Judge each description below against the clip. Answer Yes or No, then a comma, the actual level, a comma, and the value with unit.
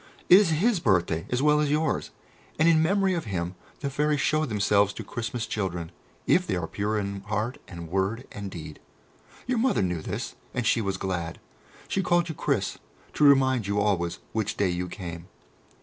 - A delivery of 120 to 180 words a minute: No, average, 190 wpm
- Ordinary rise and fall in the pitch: No, wide, 8.2 semitones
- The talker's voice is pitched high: No, low, 105 Hz